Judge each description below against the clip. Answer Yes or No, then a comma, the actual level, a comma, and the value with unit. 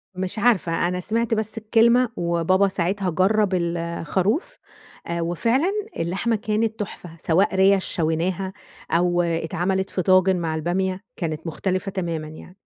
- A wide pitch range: No, average, 3.3 semitones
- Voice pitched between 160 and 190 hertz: Yes, medium, 185 Hz